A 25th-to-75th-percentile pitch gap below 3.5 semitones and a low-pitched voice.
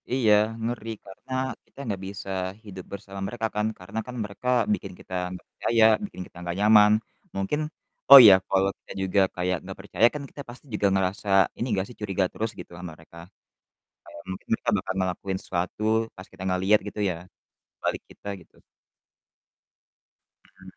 Yes: average, 2.7 semitones; low, 100 Hz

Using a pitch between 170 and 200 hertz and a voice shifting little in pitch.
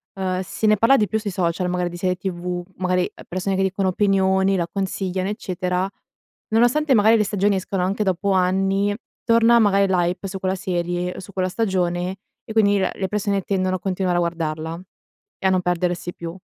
Yes: high, 190 Hz; narrow, 1.9 semitones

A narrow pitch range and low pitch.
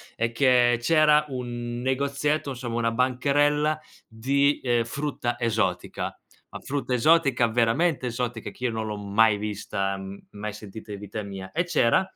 No: average, 4.1 semitones; low, 120 Hz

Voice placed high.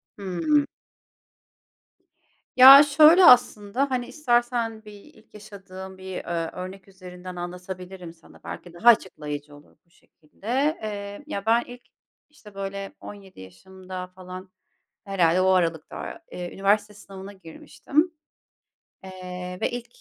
Yes: high, 195 Hz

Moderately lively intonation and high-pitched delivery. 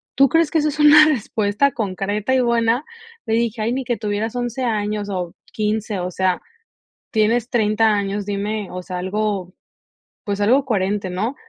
Yes: average, 3.1 semitones; high, 215 Hz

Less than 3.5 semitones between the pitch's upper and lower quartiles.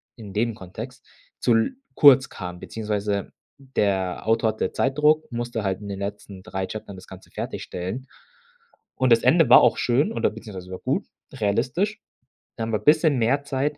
No: average, 5.1 semitones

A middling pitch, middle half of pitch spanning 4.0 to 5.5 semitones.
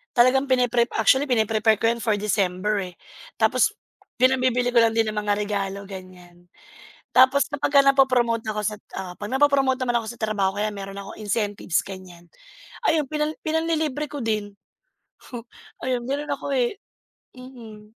No: high, 230 Hz; average, 4.3 semitones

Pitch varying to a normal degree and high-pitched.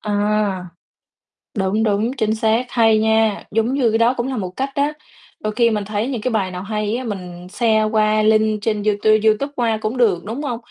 No: narrow, 1.8 semitones; high, 220 Hz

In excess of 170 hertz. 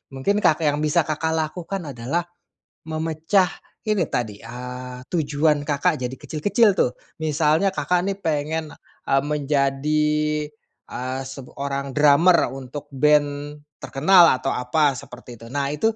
No: medium, 150 Hz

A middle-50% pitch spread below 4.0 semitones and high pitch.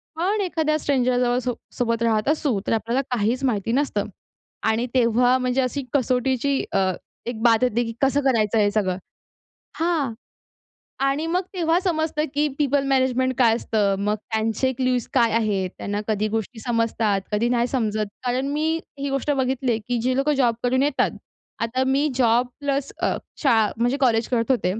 Yes: average, 3.4 semitones; very high, 250 Hz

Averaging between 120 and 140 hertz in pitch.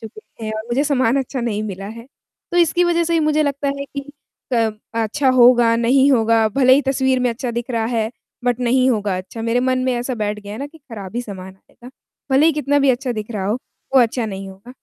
No: high, 240 Hz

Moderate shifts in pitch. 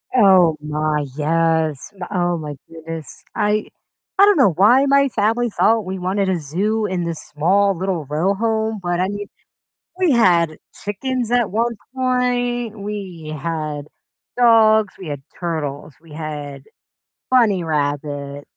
No: wide, 6.0 semitones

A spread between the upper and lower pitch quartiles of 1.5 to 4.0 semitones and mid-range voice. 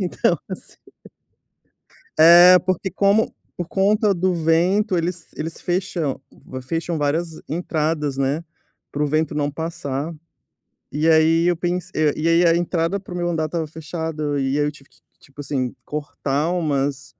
Yes: average, 2.9 semitones; medium, 165 Hz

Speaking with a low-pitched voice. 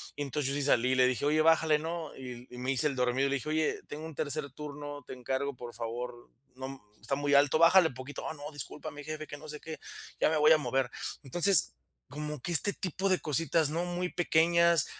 No: medium, 145 Hz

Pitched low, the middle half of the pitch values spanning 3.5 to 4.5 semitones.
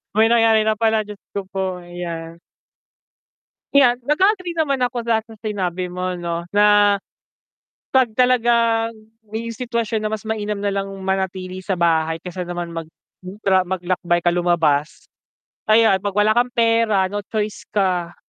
No: high, 205 Hz; average, 4.0 semitones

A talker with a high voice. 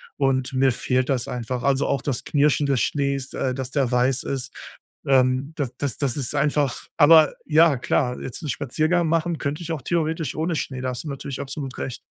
No: medium, 140 Hz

